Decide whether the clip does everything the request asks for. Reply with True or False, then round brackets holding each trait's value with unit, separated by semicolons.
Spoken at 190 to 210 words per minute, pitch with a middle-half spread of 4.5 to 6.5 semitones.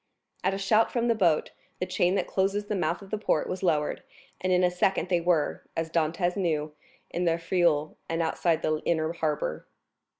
False (200 wpm; 2.9 semitones)